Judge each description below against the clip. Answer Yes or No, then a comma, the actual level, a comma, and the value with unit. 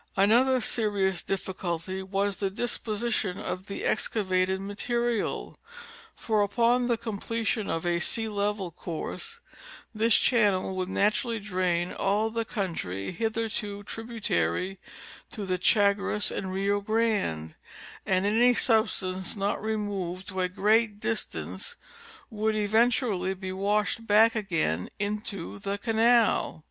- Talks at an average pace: No, slow, 120 wpm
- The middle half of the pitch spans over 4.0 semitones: No, average, 2.9 semitones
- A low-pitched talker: No, high, 205 Hz